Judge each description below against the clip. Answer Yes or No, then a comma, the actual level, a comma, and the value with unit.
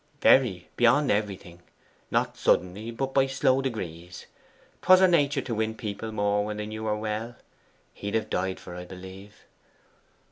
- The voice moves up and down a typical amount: Yes, average, 4.1 semitones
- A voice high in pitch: No, low, 110 Hz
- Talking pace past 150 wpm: Yes, average, 165 wpm